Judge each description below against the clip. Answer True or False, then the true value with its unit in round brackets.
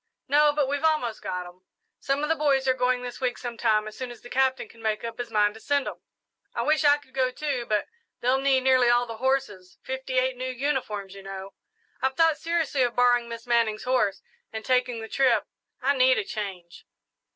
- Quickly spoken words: True (220 wpm)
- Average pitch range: True (3.3 semitones)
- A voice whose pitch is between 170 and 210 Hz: False (250 Hz)